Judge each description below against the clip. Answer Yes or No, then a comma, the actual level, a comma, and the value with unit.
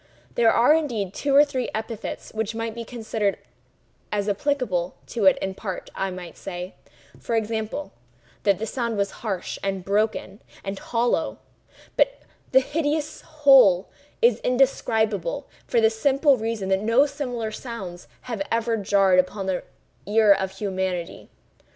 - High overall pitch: Yes, high, 220 Hz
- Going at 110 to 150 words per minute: Yes, average, 145 wpm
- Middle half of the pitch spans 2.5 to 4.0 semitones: No, average, 4.4 semitones